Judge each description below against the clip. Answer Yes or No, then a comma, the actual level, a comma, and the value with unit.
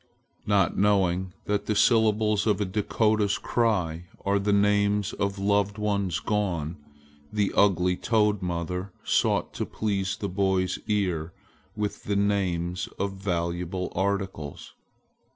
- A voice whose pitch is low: Yes, low, 100 Hz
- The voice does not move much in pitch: Yes, narrow, 2.2 semitones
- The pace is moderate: No, slow, 125 wpm